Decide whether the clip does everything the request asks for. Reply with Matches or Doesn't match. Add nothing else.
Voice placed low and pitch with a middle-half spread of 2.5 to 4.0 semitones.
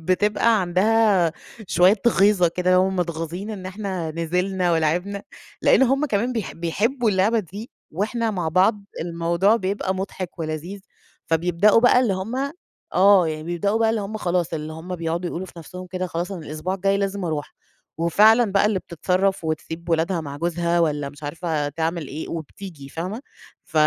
Doesn't match